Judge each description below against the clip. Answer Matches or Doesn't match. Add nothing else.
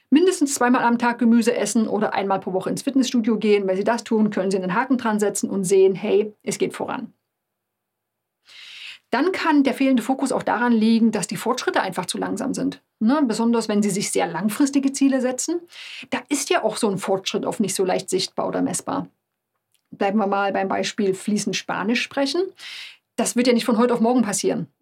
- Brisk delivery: Matches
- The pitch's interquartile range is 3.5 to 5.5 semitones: Matches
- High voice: Matches